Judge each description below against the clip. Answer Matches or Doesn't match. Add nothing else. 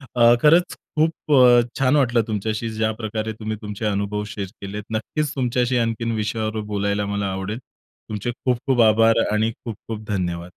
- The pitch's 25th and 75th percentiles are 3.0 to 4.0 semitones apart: Doesn't match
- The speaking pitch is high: Doesn't match